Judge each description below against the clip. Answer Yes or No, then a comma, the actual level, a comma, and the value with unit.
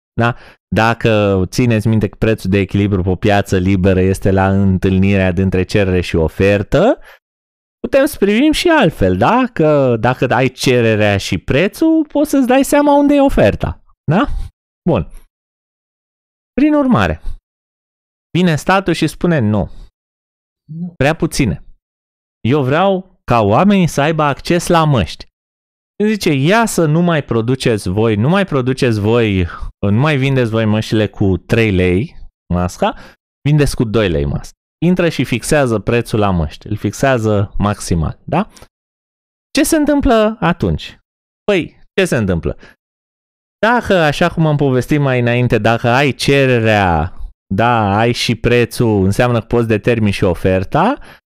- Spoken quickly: No, average, 140 wpm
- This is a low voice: Yes, low, 120 Hz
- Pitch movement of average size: No, wide, 8.1 semitones